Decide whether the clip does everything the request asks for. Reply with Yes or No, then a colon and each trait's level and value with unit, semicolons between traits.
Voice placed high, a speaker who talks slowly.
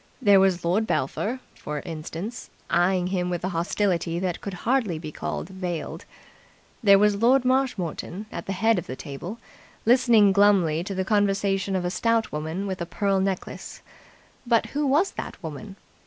No: high, 195 Hz; average, 170 wpm